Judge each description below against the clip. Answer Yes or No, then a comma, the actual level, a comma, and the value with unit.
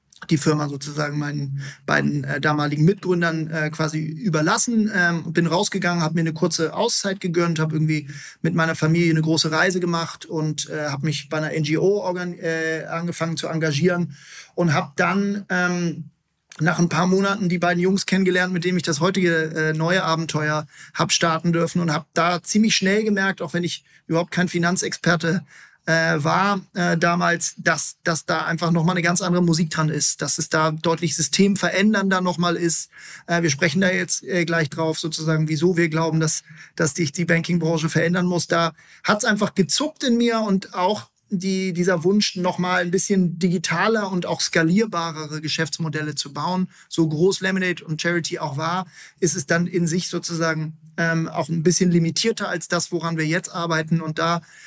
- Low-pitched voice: No, medium, 170 Hz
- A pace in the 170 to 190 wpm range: Yes, average, 185 wpm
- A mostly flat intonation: Yes, narrow, 2.2 semitones